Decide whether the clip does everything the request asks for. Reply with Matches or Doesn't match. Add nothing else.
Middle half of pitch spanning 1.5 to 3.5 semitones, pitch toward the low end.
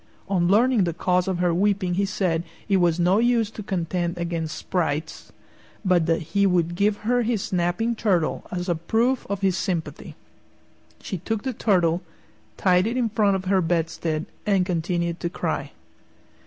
Doesn't match